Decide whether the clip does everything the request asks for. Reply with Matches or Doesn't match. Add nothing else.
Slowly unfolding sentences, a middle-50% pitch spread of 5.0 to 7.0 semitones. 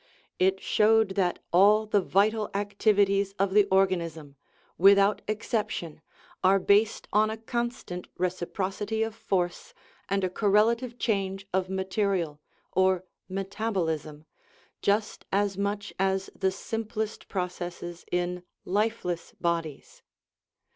Doesn't match